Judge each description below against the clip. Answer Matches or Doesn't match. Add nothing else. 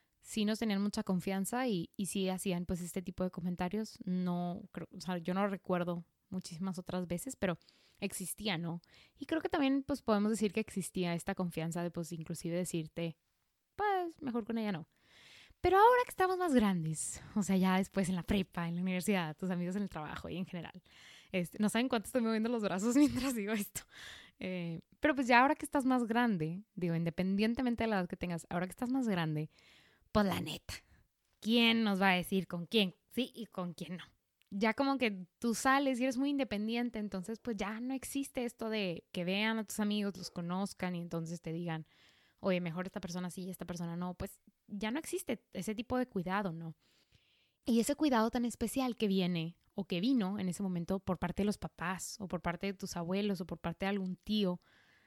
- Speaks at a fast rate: Matches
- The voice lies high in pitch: Matches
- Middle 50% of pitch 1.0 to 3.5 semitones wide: Doesn't match